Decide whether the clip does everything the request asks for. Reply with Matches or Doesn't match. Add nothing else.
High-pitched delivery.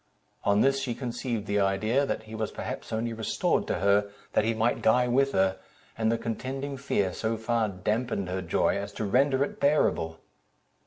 Doesn't match